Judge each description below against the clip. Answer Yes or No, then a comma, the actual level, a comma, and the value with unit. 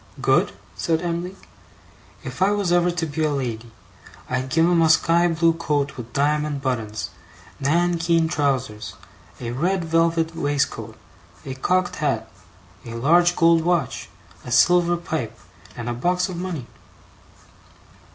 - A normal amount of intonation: Yes, average, 4.4 semitones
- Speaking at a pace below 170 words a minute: Yes, average, 140 wpm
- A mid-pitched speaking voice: Yes, medium, 160 Hz